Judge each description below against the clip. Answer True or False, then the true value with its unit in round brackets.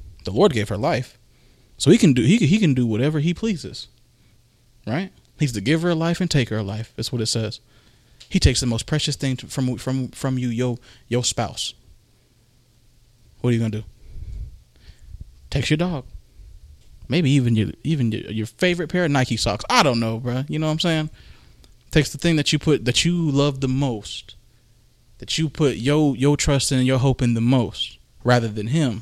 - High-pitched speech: False (125 Hz)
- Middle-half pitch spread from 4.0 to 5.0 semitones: True (4.3 semitones)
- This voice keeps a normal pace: False (210 wpm)